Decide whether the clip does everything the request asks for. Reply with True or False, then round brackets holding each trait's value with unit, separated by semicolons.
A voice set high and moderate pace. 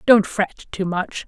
True (195 Hz; 190 wpm)